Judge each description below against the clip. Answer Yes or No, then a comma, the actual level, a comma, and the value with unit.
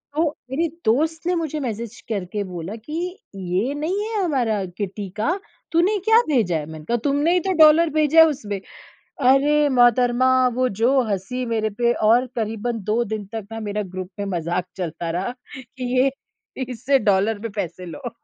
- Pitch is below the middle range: No, high, 235 Hz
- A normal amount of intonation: No, wide, 6.0 semitones